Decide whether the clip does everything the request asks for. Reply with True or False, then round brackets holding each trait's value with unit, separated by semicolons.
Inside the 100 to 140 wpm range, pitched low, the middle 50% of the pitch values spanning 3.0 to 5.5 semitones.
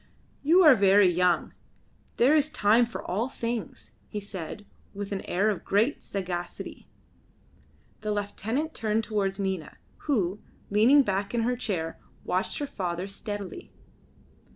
False (135 wpm; 205 Hz; 3.7 semitones)